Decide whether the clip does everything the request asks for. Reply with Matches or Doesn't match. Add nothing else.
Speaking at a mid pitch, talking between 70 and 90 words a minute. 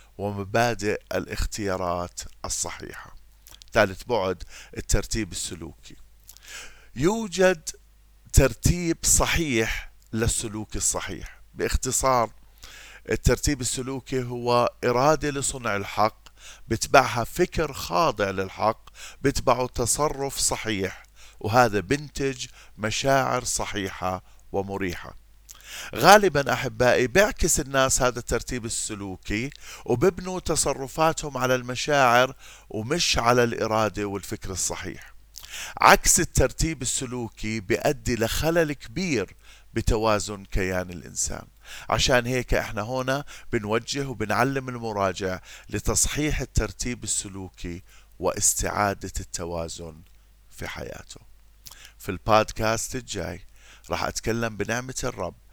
Doesn't match